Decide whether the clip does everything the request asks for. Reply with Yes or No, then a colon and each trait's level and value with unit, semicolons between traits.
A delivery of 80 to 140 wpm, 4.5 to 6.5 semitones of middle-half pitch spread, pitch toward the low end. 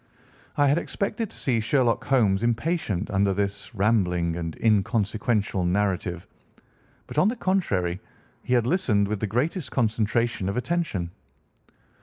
Yes: slow, 135 wpm; average, 5.2 semitones; low, 110 Hz